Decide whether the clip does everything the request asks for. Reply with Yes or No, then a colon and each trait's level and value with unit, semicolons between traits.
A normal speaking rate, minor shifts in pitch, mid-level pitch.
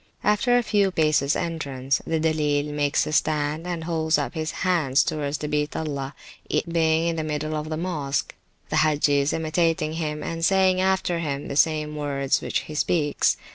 Yes: average, 180 wpm; narrow, 2.1 semitones; medium, 155 Hz